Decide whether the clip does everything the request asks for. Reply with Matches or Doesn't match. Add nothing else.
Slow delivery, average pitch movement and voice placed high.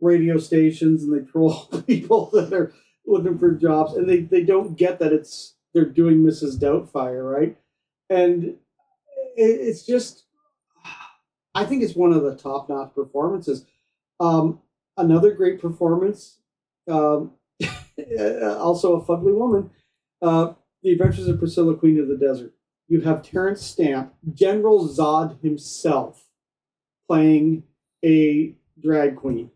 Doesn't match